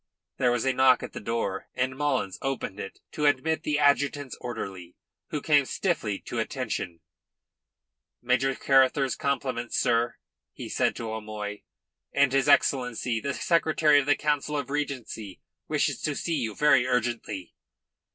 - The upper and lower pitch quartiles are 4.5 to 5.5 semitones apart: No, average, 3.9 semitones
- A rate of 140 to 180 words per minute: Yes, average, 150 wpm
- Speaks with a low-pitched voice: Yes, low, 130 Hz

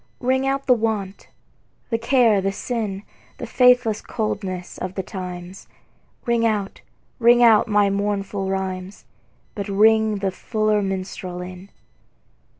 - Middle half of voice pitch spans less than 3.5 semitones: Yes, average, 3.0 semitones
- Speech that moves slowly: Yes, slow, 130 wpm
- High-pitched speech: Yes, high, 205 Hz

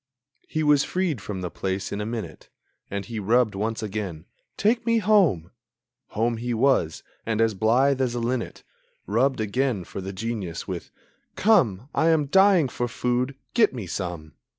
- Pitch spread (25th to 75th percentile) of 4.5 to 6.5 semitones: Yes, wide, 5.6 semitones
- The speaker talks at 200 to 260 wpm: No, average, 170 wpm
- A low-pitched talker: Yes, low, 115 Hz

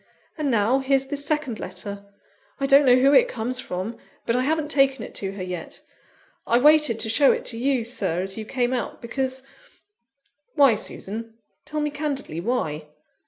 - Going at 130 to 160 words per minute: No, average, 185 wpm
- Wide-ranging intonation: No, average, 4.2 semitones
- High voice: Yes, very high, 255 Hz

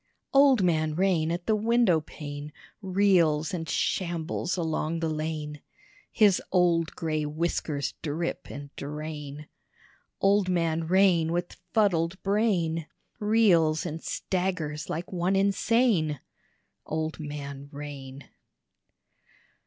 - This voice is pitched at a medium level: Yes, medium, 165 Hz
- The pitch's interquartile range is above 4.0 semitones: No, average, 3.6 semitones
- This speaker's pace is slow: Yes, slow, 105 wpm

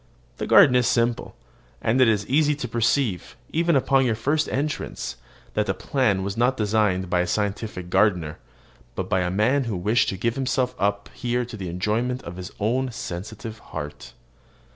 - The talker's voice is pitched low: Yes, low, 110 Hz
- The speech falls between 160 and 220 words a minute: Yes, average, 180 wpm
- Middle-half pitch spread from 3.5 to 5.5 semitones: Yes, average, 4.6 semitones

